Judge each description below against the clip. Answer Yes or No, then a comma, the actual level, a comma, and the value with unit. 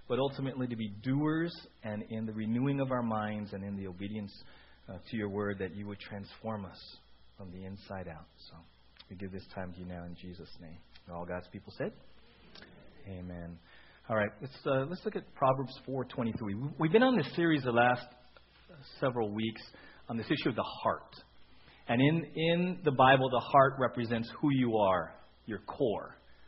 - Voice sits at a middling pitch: No, low, 110 Hz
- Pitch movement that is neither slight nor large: No, wide, 5.8 semitones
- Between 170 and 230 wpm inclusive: Yes, average, 185 wpm